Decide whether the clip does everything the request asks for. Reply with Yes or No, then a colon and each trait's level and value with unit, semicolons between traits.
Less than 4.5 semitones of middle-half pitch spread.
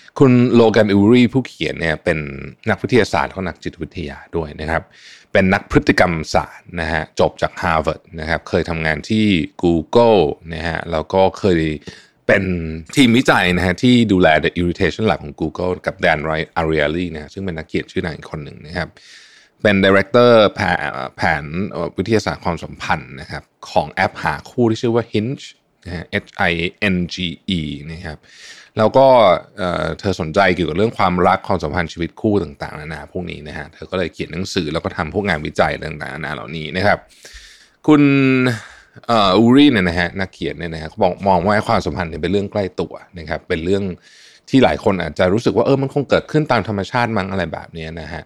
No: average, 4.8 semitones